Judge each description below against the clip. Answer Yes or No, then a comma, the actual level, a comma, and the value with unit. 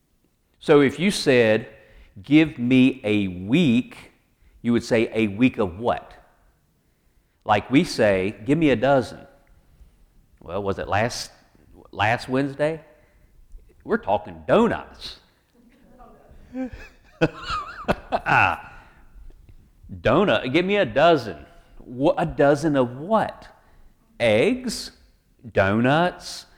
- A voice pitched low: Yes, low, 130 Hz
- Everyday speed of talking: No, slow, 95 wpm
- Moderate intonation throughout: No, wide, 8.0 semitones